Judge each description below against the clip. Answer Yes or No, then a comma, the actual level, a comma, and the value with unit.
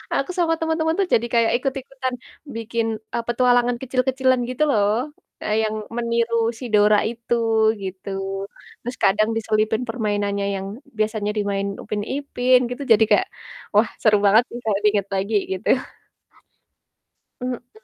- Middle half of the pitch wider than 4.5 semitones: No, average, 3.3 semitones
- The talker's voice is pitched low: No, high, 230 Hz